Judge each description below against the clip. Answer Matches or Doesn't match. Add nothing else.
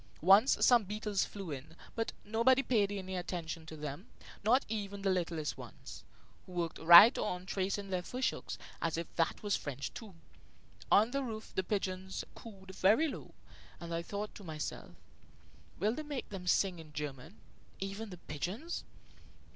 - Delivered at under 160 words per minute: Doesn't match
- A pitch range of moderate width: Matches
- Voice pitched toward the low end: Doesn't match